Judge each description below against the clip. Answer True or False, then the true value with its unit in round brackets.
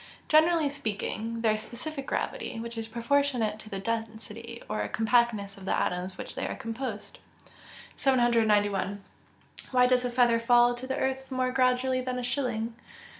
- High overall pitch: True (235 Hz)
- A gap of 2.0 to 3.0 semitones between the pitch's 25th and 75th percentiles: True (2.6 semitones)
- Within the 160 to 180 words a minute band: True (165 wpm)